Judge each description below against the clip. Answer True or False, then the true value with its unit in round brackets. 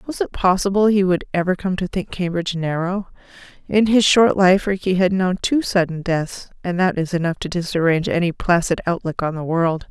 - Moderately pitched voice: True (180 Hz)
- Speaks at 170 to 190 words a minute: False (200 wpm)